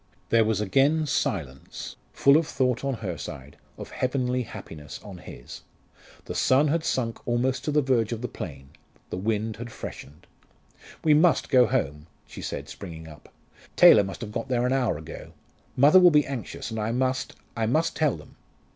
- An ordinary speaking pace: Yes, average, 180 wpm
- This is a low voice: Yes, low, 120 Hz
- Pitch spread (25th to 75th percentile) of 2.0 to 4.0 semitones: No, wide, 5.6 semitones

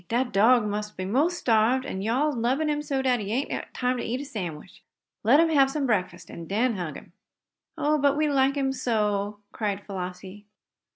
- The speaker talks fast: Yes, fast, 210 wpm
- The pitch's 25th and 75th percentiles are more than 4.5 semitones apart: Yes, average, 5.1 semitones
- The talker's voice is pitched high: Yes, high, 240 Hz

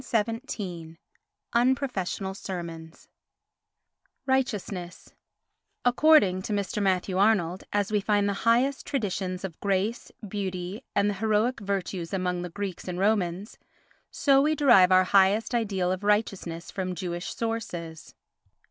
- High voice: Yes, high, 195 Hz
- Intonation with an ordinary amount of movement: Yes, average, 3.4 semitones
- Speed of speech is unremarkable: No, slow, 120 wpm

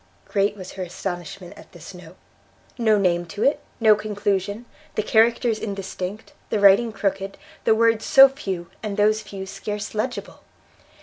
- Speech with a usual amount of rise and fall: No, narrow, 2.1 semitones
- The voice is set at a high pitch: Yes, high, 205 Hz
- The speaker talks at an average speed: Yes, average, 150 wpm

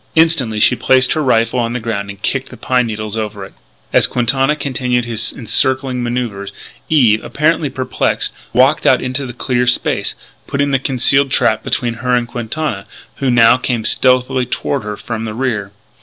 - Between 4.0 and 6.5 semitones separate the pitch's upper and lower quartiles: No, average, 2.7 semitones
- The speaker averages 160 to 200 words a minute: Yes, average, 175 wpm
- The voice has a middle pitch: No, low, 125 Hz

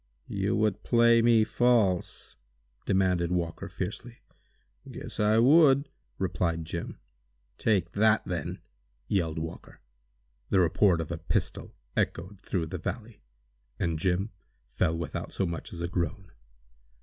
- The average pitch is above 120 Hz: No, very low, 95 Hz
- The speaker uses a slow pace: Yes, slow, 125 wpm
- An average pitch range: Yes, average, 4.2 semitones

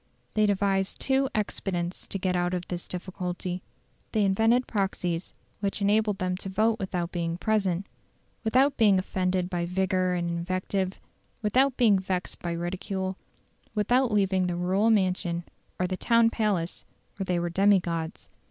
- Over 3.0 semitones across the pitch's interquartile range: No, average, 2.7 semitones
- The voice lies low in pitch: No, high, 190 Hz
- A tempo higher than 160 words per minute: No, average, 150 wpm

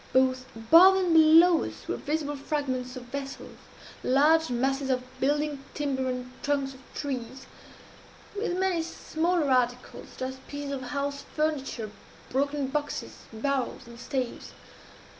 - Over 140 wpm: No, slow, 135 wpm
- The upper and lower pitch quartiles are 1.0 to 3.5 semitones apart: Yes, average, 2.9 semitones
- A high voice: Yes, very high, 280 Hz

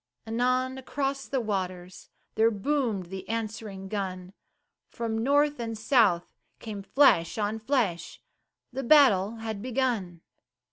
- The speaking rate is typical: No, slow, 120 wpm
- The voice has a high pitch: Yes, high, 225 Hz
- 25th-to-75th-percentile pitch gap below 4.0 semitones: No, average, 4.9 semitones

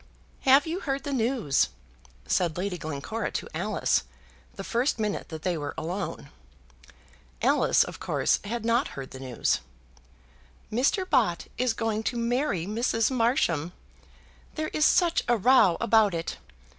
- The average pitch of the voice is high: Yes, high, 225 Hz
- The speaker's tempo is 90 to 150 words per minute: Yes, average, 145 wpm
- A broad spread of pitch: Yes, wide, 6.6 semitones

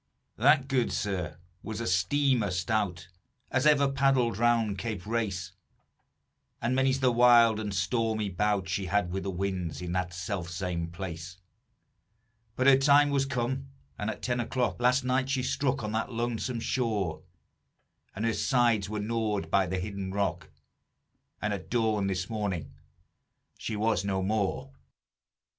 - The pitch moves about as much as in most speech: Yes, average, 4.7 semitones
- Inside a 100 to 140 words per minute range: No, average, 150 wpm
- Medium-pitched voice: No, low, 110 Hz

